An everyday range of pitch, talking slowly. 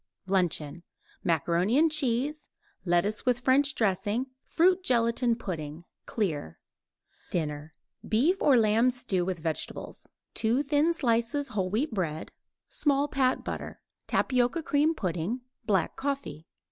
No: wide, 7.5 semitones; slow, 120 wpm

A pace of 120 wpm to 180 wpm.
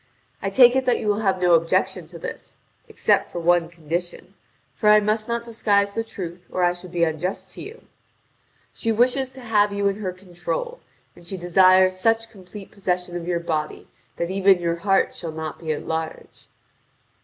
No: average, 190 wpm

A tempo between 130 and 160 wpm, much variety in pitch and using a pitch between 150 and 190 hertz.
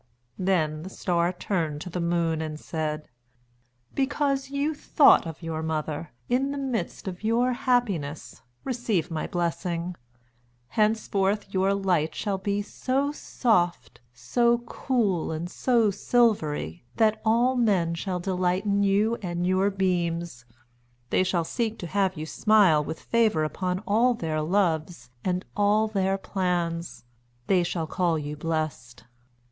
No: average, 140 wpm; average, 4.7 semitones; medium, 185 Hz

